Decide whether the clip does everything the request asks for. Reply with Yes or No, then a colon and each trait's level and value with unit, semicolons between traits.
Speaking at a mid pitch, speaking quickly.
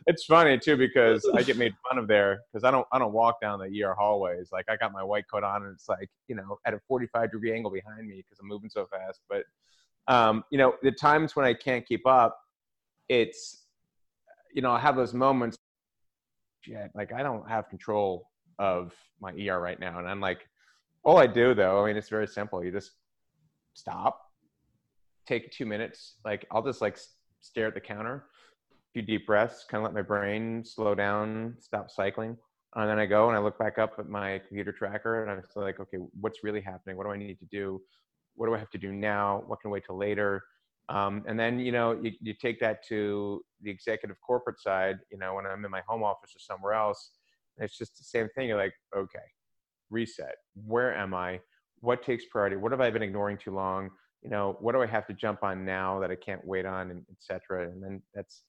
No: low, 105 Hz; fast, 225 wpm